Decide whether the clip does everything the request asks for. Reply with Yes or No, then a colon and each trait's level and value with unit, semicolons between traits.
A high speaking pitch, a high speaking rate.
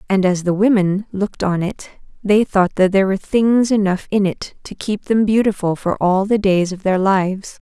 Yes: high, 195 Hz; fast, 210 wpm